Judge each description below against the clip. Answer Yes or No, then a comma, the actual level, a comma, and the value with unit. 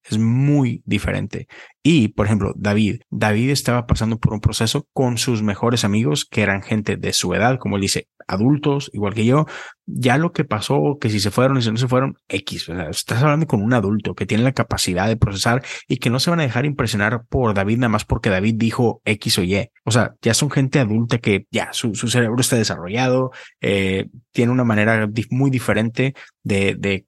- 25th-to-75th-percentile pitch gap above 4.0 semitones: No, average, 3.5 semitones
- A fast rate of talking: Yes, fast, 215 wpm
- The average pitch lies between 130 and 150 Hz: No, low, 115 Hz